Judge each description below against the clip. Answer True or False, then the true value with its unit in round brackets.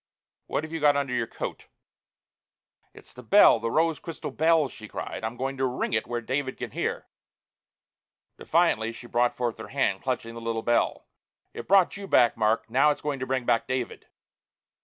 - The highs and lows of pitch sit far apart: False (4.2 semitones)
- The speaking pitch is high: False (130 Hz)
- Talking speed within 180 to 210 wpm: True (190 wpm)